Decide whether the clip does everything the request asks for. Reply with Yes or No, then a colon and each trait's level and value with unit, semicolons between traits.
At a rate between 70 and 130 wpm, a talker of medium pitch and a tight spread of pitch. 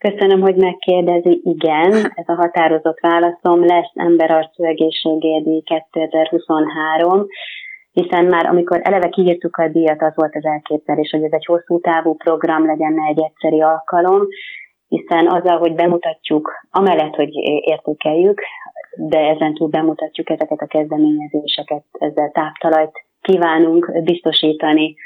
Yes: average, 120 wpm; medium, 160 Hz; narrow, 1.8 semitones